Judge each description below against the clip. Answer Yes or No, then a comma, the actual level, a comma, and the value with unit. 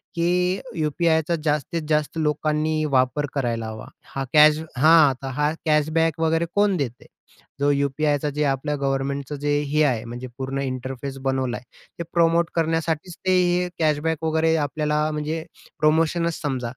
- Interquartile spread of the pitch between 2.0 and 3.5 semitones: Yes, average, 2.8 semitones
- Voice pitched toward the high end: No, medium, 150 Hz